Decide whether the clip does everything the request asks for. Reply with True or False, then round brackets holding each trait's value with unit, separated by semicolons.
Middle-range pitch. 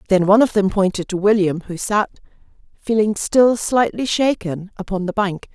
False (205 Hz)